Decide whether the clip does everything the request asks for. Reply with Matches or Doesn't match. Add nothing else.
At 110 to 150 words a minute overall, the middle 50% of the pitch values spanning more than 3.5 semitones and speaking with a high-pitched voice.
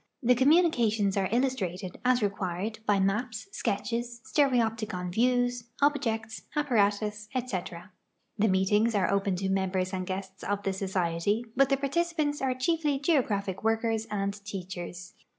Matches